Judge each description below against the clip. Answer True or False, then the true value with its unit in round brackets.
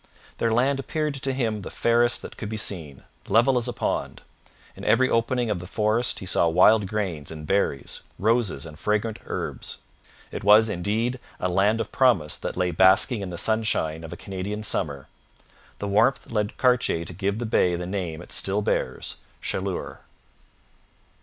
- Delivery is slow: False (180 wpm)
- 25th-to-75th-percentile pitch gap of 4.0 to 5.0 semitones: True (4.5 semitones)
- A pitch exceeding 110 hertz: False (105 Hz)